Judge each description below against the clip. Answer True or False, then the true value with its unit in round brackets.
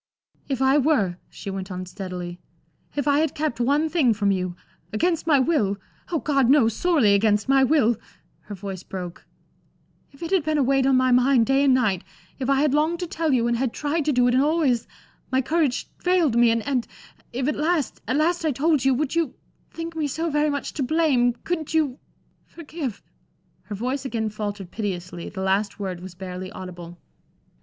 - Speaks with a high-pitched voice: True (260 Hz)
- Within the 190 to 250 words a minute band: True (200 wpm)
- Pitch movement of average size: False (6.6 semitones)